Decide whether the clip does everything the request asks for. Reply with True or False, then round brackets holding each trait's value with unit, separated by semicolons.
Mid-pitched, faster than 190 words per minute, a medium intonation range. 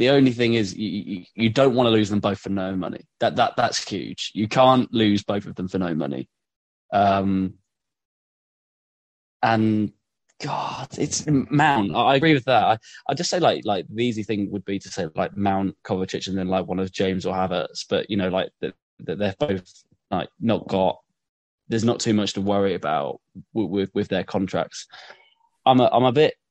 False (100 Hz; 205 wpm; 3.3 semitones)